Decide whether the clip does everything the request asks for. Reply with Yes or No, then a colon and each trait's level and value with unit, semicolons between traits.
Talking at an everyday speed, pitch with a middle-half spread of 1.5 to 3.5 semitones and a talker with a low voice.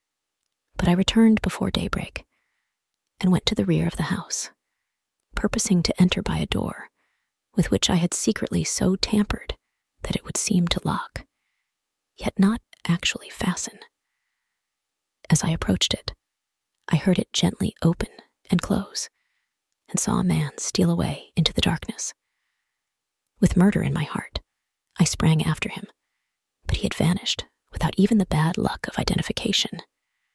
No: average, 150 wpm; average, 3.2 semitones; medium, 185 Hz